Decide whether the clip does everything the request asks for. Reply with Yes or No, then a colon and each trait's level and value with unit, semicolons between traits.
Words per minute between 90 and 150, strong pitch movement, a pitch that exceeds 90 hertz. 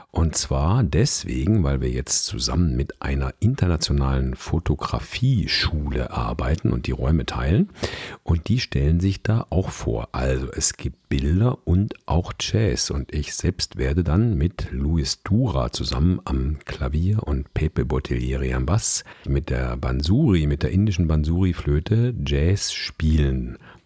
No: average, 140 wpm; wide, 5.8 semitones; very low, 75 Hz